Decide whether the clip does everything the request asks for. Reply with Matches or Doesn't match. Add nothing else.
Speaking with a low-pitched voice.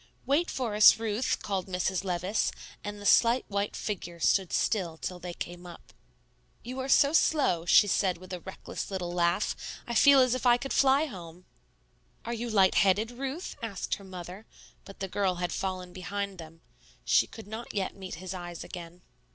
Doesn't match